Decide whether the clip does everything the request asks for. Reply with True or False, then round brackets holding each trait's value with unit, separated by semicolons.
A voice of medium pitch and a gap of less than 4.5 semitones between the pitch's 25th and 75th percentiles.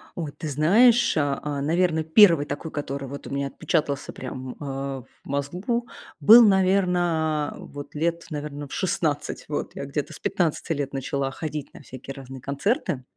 True (150 Hz; 3.7 semitones)